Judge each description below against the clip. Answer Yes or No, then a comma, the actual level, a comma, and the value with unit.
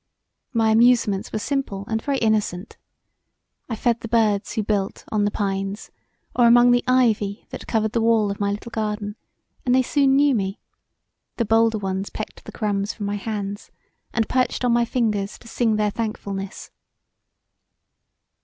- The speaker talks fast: No, average, 165 wpm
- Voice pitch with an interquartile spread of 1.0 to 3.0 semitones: Yes, narrow, 2.6 semitones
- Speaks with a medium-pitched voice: No, high, 220 Hz